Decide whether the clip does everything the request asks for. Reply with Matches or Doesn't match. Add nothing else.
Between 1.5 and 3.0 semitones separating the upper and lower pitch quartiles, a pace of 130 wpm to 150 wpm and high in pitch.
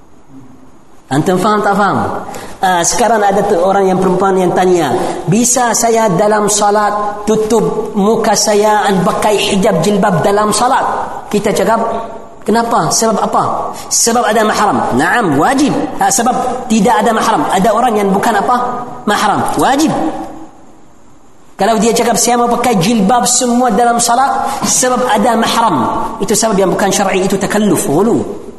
Matches